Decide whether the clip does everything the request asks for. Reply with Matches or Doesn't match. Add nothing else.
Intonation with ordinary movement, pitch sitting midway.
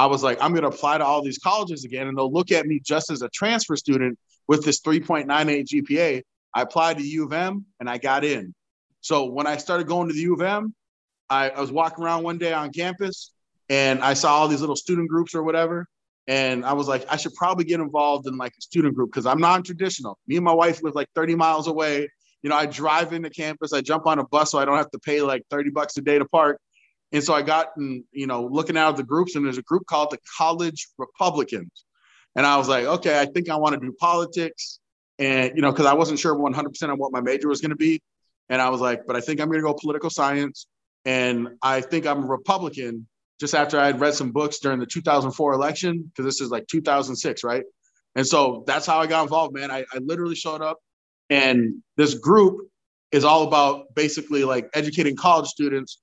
Matches